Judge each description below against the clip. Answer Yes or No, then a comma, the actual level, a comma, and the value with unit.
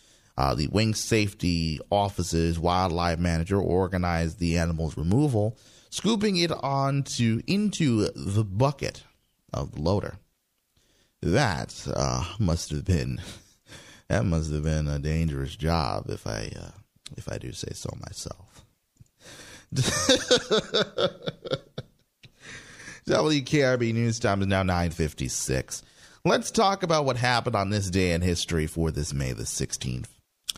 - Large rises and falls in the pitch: Yes, wide, 6.3 semitones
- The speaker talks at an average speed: No, slow, 125 wpm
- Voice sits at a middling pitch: No, very low, 95 Hz